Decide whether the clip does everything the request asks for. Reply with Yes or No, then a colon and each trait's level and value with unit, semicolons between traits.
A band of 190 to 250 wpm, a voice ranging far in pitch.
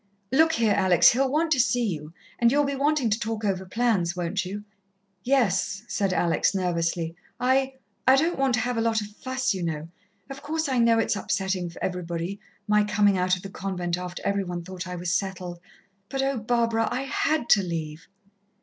Yes: average, 200 wpm; wide, 5.8 semitones